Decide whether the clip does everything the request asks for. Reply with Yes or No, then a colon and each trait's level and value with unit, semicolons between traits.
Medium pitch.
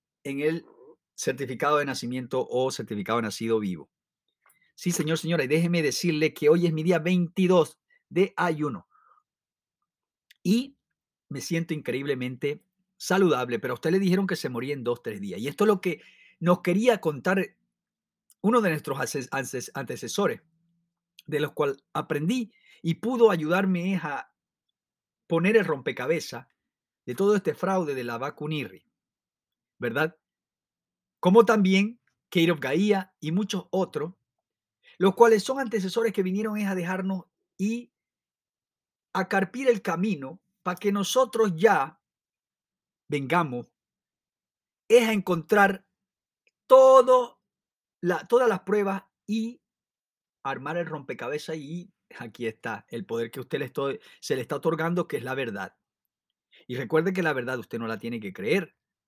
Yes: medium, 180 Hz